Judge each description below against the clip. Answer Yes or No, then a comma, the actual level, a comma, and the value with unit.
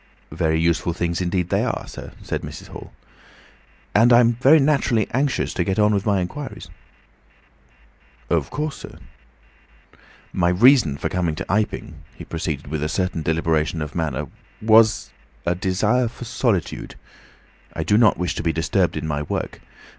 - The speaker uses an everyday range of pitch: No, wide, 5.7 semitones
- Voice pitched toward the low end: Yes, very low, 90 Hz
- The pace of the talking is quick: No, average, 160 wpm